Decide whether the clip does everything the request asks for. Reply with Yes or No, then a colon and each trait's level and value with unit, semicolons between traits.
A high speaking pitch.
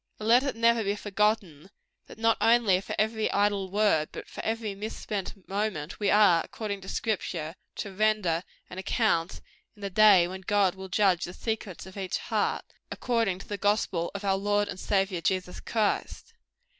Yes: high, 200 Hz